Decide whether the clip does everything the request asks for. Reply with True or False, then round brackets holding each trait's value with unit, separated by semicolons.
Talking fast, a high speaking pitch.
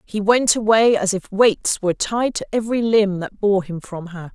True (220 wpm; 205 Hz)